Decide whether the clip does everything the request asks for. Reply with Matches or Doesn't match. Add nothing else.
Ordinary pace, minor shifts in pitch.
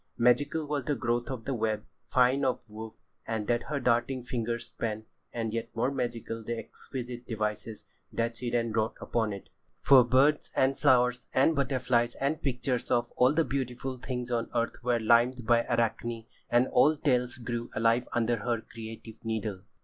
Matches